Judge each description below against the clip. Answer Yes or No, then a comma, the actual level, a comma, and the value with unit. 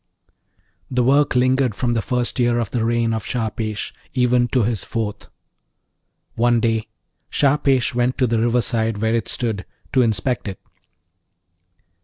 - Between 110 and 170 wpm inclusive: Yes, average, 145 wpm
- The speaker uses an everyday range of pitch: No, narrow, 1.9 semitones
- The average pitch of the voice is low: Yes, low, 120 Hz